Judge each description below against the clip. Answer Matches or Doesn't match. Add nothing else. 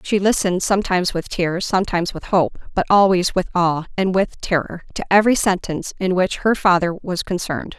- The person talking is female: Matches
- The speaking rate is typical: Matches